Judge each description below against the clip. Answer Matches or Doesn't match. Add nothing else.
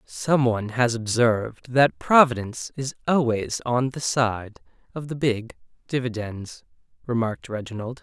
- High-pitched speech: Doesn't match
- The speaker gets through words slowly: Matches